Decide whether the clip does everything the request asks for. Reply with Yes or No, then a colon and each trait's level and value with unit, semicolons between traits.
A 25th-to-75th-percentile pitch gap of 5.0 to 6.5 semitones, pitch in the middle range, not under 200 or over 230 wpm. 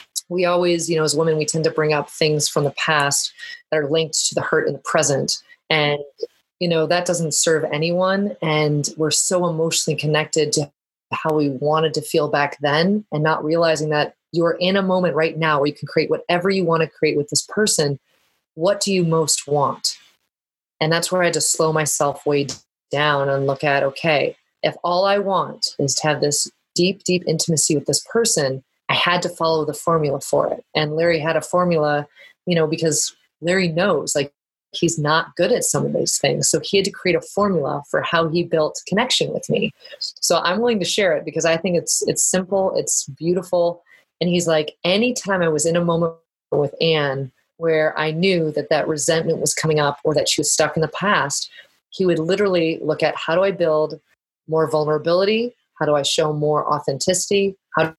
No: average, 2.7 semitones; medium, 160 Hz; fast, 205 wpm